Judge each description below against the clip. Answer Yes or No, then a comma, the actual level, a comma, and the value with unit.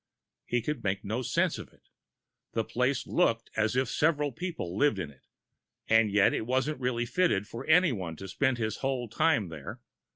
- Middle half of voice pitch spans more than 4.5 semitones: Yes, average, 5.2 semitones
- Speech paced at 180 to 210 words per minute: Yes, average, 185 wpm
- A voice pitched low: Yes, low, 120 Hz